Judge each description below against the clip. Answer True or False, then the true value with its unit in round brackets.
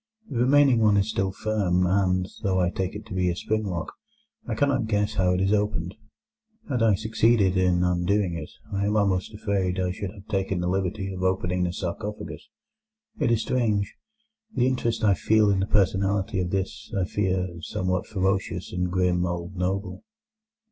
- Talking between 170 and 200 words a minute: True (185 wpm)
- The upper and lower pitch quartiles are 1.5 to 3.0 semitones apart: True (2.5 semitones)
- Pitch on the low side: True (95 Hz)